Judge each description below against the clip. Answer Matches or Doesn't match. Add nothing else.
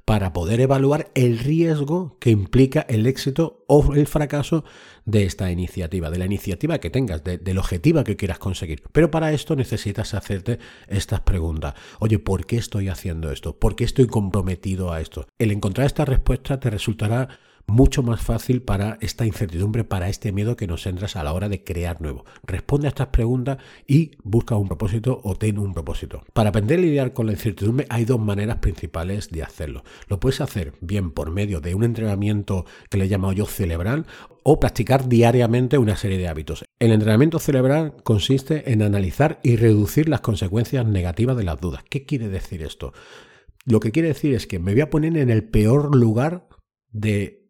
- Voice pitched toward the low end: Matches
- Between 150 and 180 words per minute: Doesn't match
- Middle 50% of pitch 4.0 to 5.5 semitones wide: Matches